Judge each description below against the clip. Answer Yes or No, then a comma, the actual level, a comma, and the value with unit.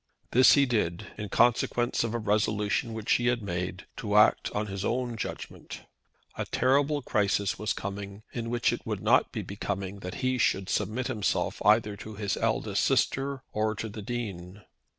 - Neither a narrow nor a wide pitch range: Yes, average, 3.2 semitones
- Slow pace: No, average, 175 wpm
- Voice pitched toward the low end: Yes, low, 105 Hz